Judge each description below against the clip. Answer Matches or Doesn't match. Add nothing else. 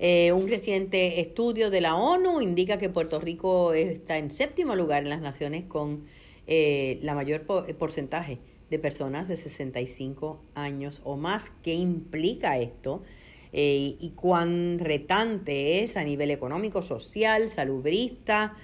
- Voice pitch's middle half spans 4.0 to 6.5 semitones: Matches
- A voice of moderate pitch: Matches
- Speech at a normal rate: Matches